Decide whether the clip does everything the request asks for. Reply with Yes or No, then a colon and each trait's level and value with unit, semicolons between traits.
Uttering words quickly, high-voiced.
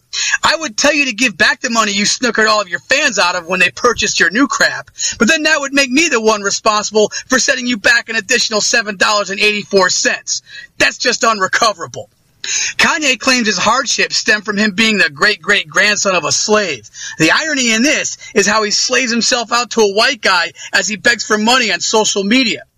Yes: fast, 215 wpm; high, 225 Hz